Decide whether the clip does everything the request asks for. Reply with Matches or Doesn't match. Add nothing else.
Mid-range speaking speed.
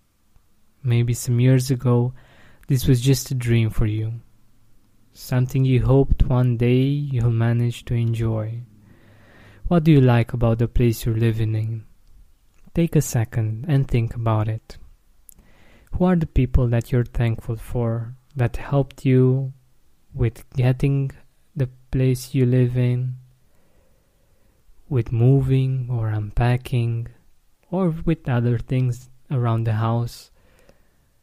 Doesn't match